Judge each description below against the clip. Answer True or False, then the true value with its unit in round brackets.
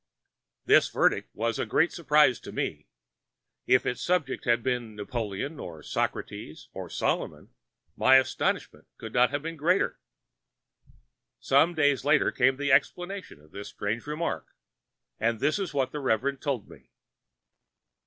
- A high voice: False (130 Hz)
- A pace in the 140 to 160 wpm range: True (145 wpm)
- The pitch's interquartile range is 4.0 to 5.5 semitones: True (4.6 semitones)